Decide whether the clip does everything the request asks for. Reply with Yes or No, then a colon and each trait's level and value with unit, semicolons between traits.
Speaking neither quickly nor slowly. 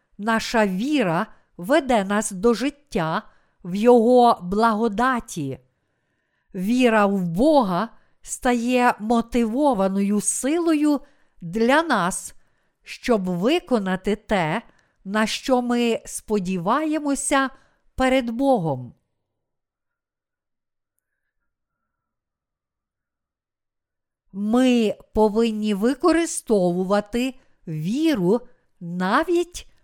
No: slow, 60 wpm